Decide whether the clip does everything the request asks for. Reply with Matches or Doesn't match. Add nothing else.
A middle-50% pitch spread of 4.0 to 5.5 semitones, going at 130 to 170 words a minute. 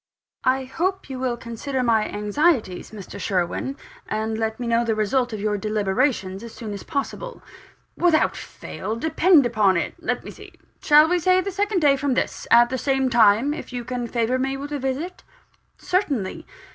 Doesn't match